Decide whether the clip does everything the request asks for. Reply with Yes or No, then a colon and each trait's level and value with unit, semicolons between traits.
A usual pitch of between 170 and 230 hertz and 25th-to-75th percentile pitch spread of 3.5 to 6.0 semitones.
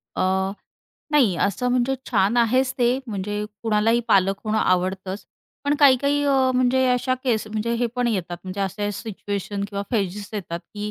Yes: high, 210 Hz; average, 4.1 semitones